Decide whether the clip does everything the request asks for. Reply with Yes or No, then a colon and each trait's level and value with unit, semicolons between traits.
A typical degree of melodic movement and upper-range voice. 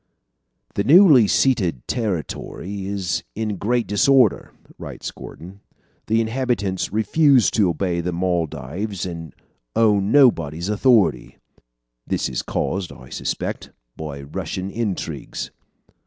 No: average, 4.8 semitones; low, 100 Hz